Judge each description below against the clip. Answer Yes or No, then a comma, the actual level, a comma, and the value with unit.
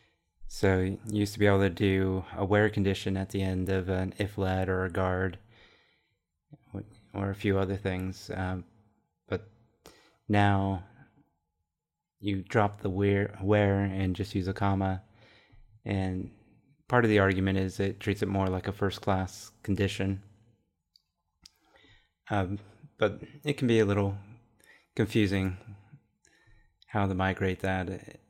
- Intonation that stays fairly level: Yes, narrow, 2.0 semitones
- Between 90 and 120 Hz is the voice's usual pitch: Yes, low, 100 Hz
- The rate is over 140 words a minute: No, slow, 135 wpm